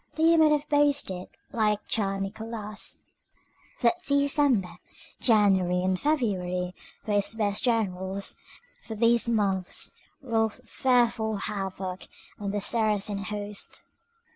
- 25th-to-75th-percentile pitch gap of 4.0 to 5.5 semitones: No, average, 3.4 semitones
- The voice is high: Yes, high, 210 Hz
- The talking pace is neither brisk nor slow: No, slow, 105 wpm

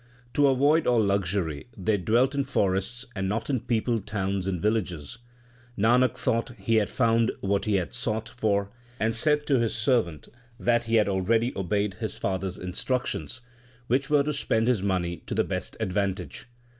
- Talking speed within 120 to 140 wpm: No, average, 175 wpm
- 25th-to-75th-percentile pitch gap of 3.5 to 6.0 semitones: Yes, average, 4.0 semitones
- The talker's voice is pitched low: Yes, low, 110 Hz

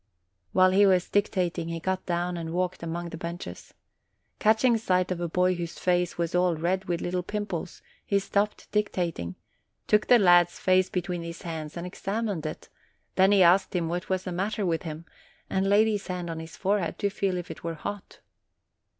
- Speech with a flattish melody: Yes, narrow, 2.3 semitones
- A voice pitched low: No, medium, 180 Hz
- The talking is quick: No, average, 195 wpm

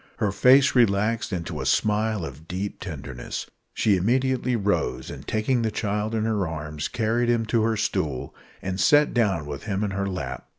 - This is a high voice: No, low, 105 Hz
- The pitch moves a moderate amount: Yes, average, 3.7 semitones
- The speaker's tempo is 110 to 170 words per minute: No, average, 180 wpm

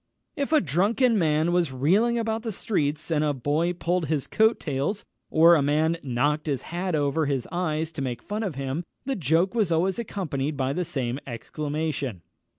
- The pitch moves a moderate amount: Yes, average, 4.6 semitones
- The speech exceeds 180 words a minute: Yes, average, 190 wpm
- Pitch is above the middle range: No, medium, 160 Hz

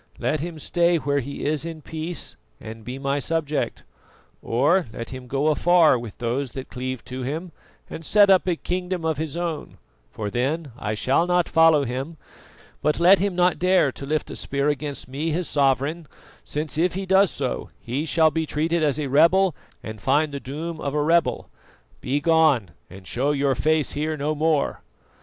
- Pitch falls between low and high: Yes, medium, 150 Hz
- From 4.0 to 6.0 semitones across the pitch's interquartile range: No, average, 3.5 semitones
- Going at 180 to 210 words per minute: Yes, average, 185 wpm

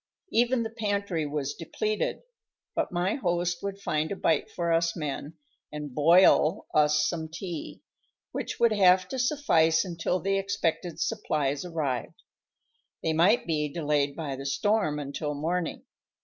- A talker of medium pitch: Yes, medium, 165 Hz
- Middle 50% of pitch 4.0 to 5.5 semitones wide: Yes, average, 4.5 semitones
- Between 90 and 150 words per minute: Yes, average, 145 wpm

